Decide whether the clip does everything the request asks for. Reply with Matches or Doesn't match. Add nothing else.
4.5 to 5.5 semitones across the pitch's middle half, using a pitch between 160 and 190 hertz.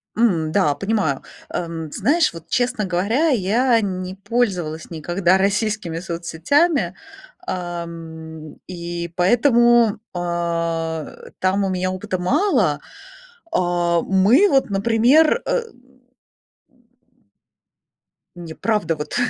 Matches